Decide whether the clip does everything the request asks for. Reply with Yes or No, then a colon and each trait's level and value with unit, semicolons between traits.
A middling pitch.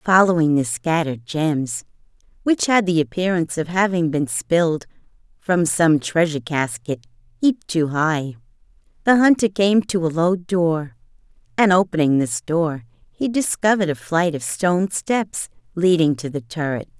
Yes: medium, 165 Hz